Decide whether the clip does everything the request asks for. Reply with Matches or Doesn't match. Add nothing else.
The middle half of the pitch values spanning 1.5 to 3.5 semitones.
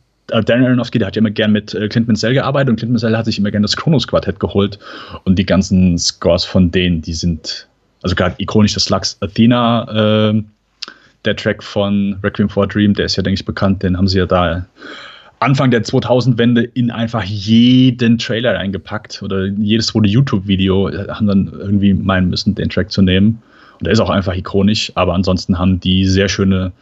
Matches